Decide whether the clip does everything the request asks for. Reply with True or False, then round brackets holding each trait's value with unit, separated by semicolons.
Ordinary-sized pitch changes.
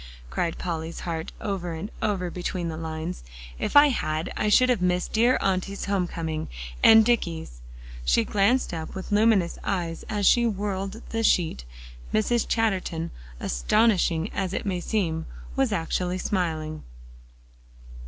True (4.4 semitones)